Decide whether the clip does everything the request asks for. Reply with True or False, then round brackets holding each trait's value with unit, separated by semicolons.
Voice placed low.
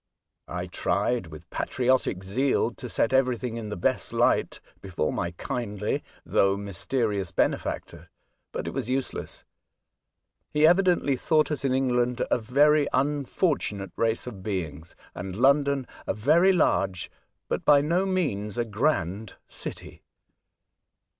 True (125 Hz)